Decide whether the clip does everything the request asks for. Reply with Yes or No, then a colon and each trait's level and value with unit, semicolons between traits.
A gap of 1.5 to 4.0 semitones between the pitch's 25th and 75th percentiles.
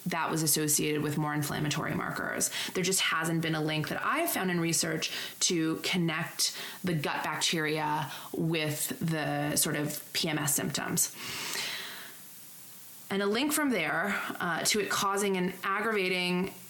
Yes: average, 3.5 semitones